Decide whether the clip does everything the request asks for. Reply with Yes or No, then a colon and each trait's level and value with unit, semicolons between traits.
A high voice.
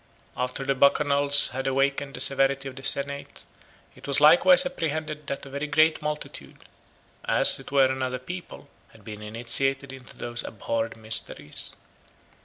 No: low, 135 Hz